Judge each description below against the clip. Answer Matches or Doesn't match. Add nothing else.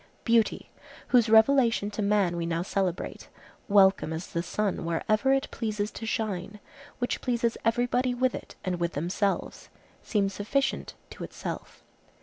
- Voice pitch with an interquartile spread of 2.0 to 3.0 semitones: Doesn't match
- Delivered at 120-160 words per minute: Matches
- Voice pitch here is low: Doesn't match